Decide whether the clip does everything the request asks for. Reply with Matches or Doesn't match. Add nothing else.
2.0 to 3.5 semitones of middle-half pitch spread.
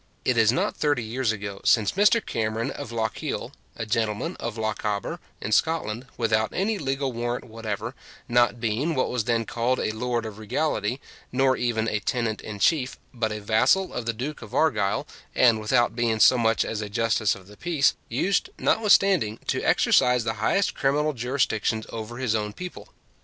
Matches